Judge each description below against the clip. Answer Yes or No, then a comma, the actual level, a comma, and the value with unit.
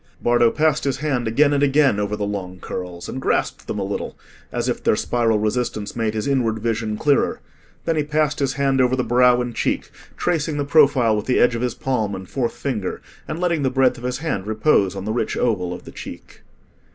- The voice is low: Yes, low, 125 Hz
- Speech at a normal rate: No, fast, 225 wpm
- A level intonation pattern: No, average, 4.6 semitones